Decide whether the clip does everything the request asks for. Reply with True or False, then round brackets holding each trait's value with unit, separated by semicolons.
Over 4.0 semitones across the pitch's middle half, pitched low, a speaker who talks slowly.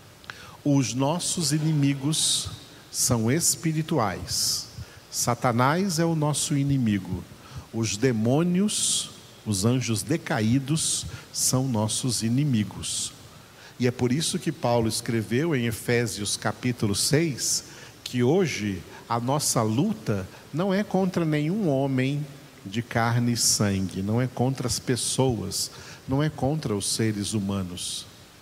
True (4.7 semitones; 125 Hz; 115 wpm)